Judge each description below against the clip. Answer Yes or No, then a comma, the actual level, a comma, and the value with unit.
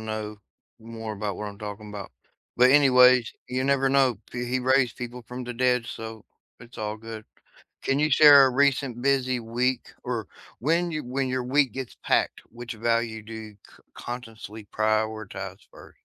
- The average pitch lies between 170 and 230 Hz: No, low, 120 Hz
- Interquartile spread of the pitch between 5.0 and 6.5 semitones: No, average, 2.8 semitones